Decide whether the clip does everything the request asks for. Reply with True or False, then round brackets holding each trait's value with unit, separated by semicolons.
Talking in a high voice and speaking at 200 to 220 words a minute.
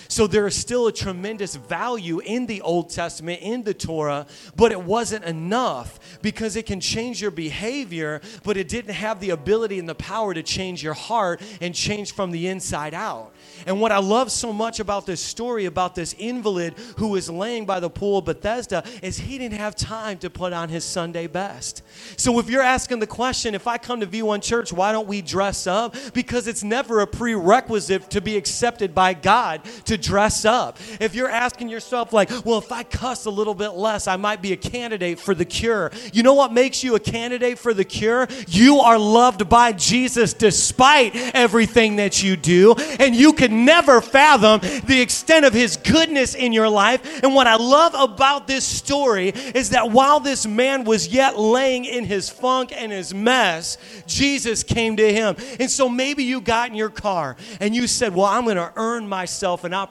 True (220 Hz; 205 wpm)